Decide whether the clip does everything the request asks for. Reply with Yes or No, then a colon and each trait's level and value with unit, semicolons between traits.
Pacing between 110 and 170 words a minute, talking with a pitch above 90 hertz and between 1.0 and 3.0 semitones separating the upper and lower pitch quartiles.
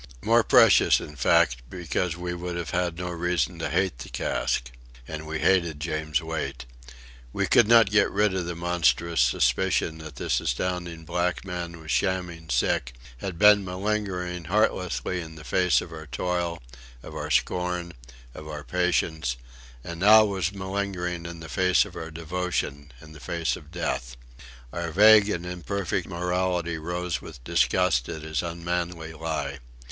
No: average, 160 wpm; very low, 85 Hz; narrow, 2.5 semitones